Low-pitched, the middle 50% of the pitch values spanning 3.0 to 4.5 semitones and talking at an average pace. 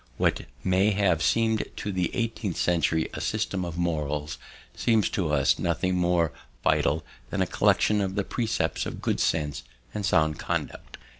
Yes: very low, 90 Hz; average, 4.2 semitones; average, 160 wpm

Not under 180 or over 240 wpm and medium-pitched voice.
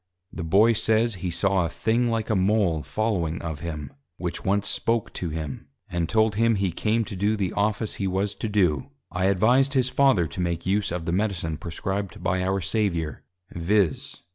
No: average, 190 wpm; very low, 95 Hz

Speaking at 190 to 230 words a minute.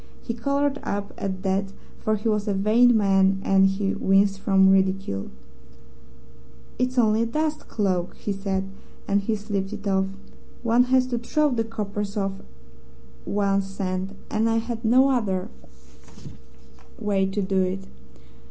No: average, 150 wpm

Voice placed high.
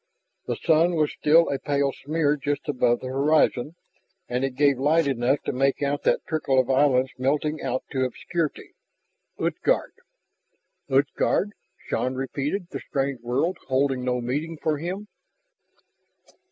No: medium, 140 Hz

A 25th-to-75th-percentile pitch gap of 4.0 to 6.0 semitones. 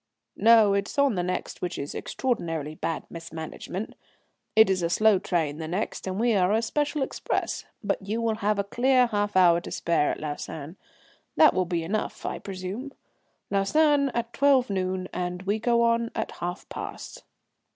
Yes: average, 4.7 semitones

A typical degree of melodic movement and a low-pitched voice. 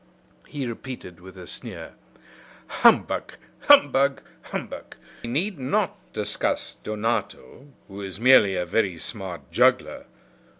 No: wide, 5.7 semitones; low, 110 Hz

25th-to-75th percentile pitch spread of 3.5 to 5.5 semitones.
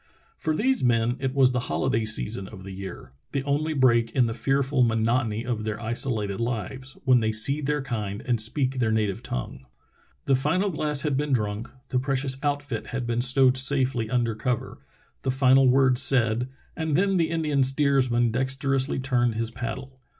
No: average, 3.1 semitones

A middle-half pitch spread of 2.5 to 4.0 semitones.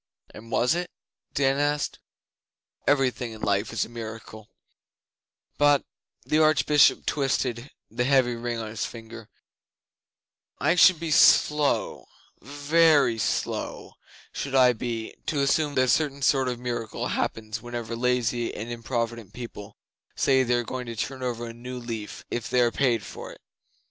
Yes: average, 3.2 semitones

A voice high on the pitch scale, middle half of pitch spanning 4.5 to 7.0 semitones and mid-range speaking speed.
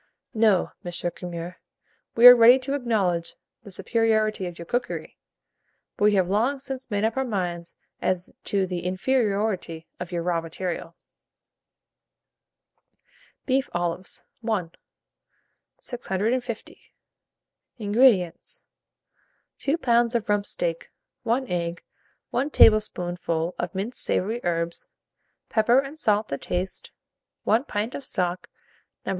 No: high, 205 Hz; average, 5.2 semitones; slow, 120 wpm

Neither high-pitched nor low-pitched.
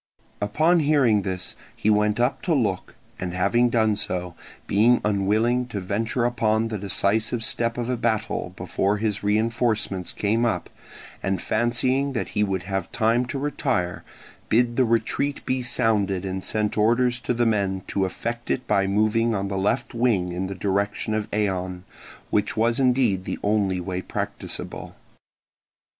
No: low, 110 Hz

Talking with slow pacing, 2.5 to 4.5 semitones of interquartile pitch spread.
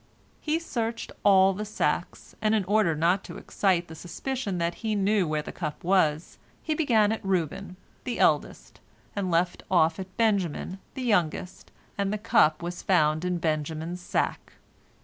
No: average, 165 wpm; average, 4.2 semitones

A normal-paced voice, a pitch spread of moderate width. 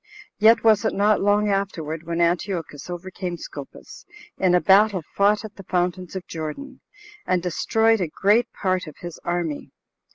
Yes: average, 160 wpm; average, 3.2 semitones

